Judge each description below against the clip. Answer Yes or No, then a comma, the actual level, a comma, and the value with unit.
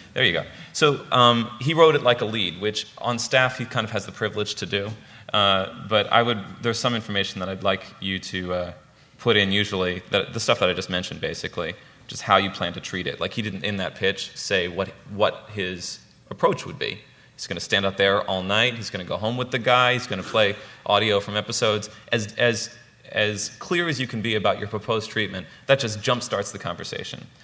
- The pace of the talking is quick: Yes, fast, 235 wpm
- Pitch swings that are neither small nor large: Yes, average, 3.7 semitones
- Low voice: Yes, low, 105 Hz